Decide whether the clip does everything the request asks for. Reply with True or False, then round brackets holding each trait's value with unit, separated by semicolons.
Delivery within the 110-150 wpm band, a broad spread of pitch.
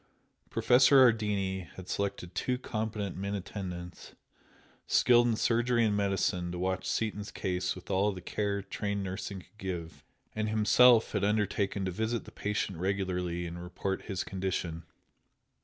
False (145 wpm; 2.8 semitones)